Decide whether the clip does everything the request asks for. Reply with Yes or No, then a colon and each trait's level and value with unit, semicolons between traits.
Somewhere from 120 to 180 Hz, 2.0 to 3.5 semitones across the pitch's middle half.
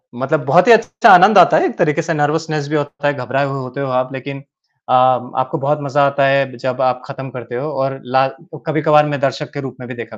Yes: medium, 140 Hz; narrow, 2.6 semitones